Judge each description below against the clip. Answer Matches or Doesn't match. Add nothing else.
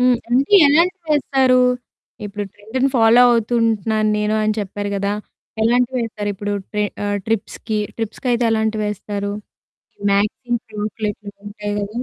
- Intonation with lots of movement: Doesn't match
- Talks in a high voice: Matches